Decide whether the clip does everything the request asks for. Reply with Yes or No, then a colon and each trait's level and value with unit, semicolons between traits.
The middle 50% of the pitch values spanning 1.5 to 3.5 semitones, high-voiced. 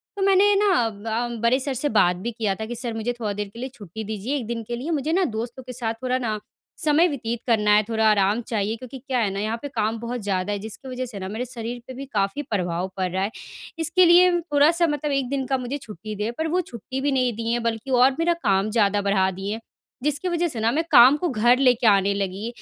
No: average, 4.3 semitones; high, 235 Hz